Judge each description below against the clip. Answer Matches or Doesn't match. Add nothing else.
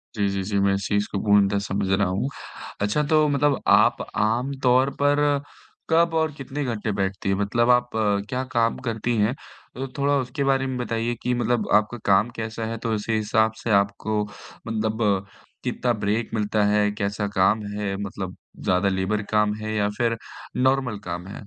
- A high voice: Doesn't match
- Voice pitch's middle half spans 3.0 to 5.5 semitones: Matches